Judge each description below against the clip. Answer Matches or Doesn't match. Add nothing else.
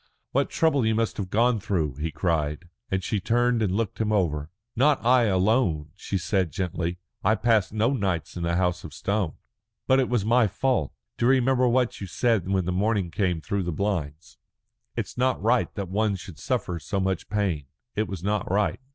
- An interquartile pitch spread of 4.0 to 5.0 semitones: Matches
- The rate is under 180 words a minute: Doesn't match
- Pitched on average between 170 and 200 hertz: Doesn't match